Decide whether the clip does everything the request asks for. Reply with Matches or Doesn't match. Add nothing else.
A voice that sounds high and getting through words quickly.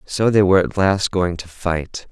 Doesn't match